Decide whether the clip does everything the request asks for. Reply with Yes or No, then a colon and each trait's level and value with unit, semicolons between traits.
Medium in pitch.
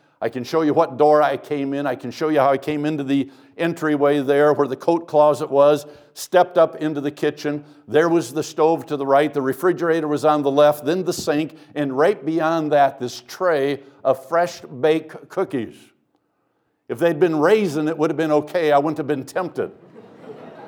Yes: medium, 150 Hz